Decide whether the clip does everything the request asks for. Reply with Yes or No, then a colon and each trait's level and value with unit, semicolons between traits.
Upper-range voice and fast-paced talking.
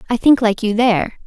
Yes: high, 225 Hz; fast, 240 wpm